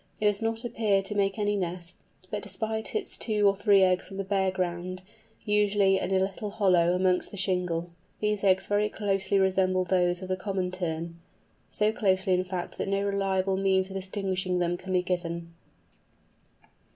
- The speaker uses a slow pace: No, average, 180 wpm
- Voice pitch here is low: No, high, 190 Hz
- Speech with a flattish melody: Yes, narrow, 1.8 semitones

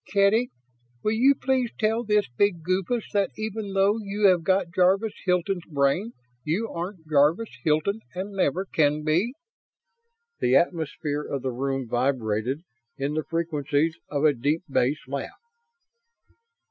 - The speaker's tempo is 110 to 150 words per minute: Yes, average, 140 wpm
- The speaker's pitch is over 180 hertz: No, medium, 170 Hz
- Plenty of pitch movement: Yes, wide, 5.9 semitones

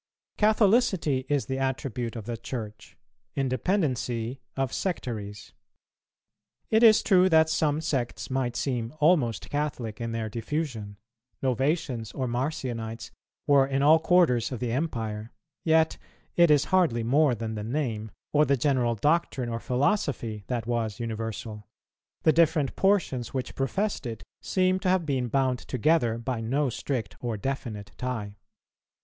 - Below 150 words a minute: Yes, average, 140 wpm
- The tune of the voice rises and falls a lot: No, average, 4.9 semitones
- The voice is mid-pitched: No, low, 130 Hz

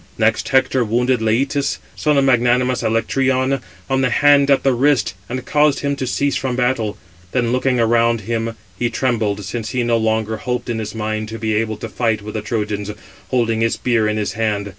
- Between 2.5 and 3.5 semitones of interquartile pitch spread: Yes, average, 2.8 semitones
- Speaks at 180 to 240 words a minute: Yes, average, 200 wpm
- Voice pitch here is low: Yes, low, 120 Hz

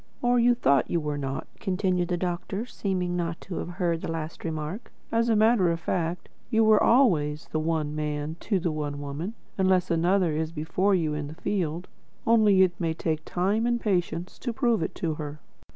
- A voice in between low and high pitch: Yes, medium, 175 Hz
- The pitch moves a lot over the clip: No, average, 4.2 semitones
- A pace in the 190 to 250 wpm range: Yes, average, 200 wpm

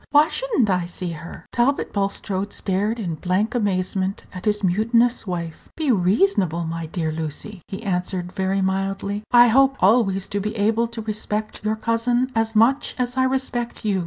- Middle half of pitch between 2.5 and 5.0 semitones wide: Yes, average, 4.0 semitones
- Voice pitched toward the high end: Yes, high, 205 Hz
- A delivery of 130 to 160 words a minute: No, average, 175 wpm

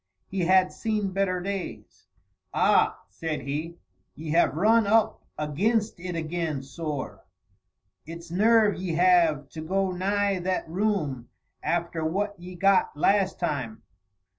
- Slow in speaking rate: Yes, slow, 130 wpm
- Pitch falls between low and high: Yes, medium, 180 Hz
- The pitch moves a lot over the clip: No, average, 3.7 semitones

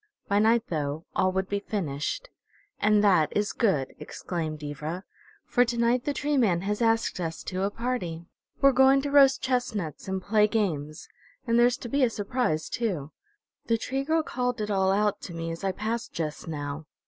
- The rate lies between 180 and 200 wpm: Yes, average, 190 wpm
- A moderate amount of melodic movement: No, wide, 6.4 semitones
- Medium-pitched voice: No, high, 205 Hz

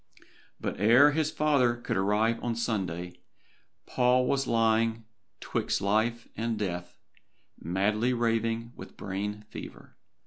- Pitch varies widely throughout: No, narrow, 2.6 semitones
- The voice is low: Yes, low, 115 Hz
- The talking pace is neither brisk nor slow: No, slow, 115 wpm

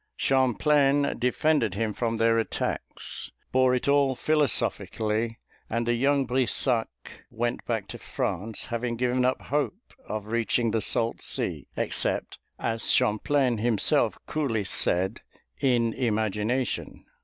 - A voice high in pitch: No, low, 120 Hz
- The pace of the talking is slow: Yes, slow, 120 wpm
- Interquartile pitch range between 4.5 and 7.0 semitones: No, average, 2.8 semitones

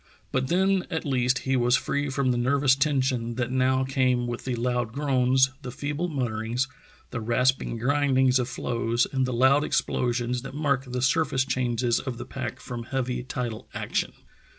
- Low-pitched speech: Yes, low, 130 Hz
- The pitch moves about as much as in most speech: No, narrow, 1.9 semitones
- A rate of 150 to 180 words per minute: Yes, average, 175 wpm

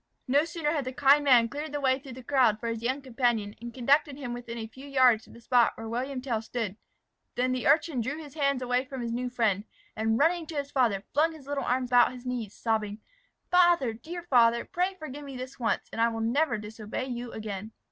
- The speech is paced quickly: Yes, fast, 230 wpm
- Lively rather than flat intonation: No, average, 3.5 semitones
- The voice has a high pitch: Yes, very high, 250 Hz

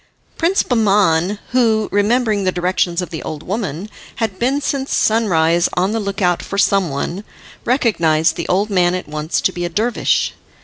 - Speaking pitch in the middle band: No, high, 195 Hz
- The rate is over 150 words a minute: Yes, average, 175 wpm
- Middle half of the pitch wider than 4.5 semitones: No, average, 4.2 semitones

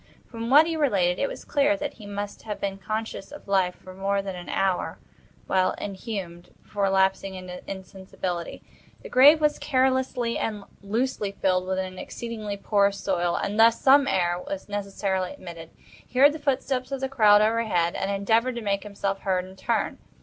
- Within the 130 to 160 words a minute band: No, average, 180 wpm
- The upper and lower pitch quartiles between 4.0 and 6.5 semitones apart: Yes, average, 4.5 semitones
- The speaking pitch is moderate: No, high, 200 Hz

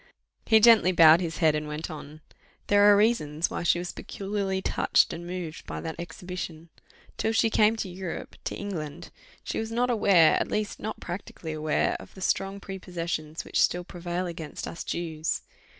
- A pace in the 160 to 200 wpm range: Yes, average, 180 wpm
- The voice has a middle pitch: Yes, medium, 175 Hz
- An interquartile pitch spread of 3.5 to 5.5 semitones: Yes, average, 3.9 semitones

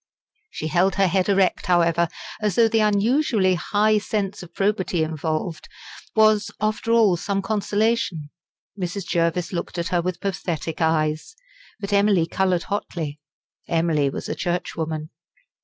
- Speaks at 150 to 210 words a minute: No, average, 140 wpm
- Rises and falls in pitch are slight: No, average, 3.7 semitones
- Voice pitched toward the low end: No, medium, 185 Hz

